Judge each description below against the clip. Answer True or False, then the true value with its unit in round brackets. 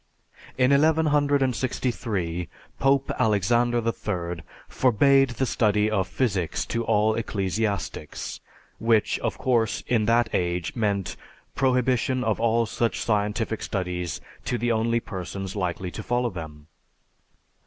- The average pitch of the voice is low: True (110 Hz)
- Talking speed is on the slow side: True (115 wpm)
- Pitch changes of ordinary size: True (4.1 semitones)